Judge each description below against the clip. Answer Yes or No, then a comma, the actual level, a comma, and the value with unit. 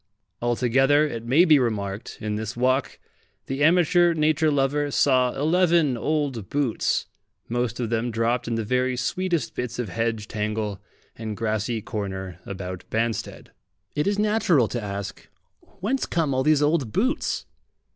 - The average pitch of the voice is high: No, low, 125 Hz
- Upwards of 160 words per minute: No, average, 145 wpm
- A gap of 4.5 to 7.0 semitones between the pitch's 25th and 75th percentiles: Yes, average, 5.3 semitones